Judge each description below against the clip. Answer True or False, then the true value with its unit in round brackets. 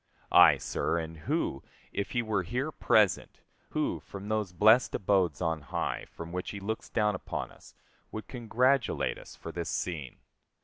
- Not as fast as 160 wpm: False (165 wpm)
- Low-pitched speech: True (100 Hz)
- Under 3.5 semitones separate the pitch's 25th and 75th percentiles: False (4.6 semitones)